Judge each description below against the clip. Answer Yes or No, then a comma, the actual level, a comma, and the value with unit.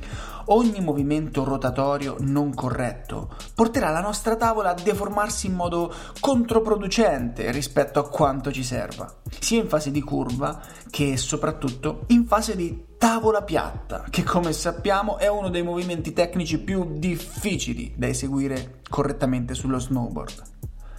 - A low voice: No, medium, 160 Hz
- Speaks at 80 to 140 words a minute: Yes, average, 130 wpm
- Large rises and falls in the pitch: Yes, wide, 6.7 semitones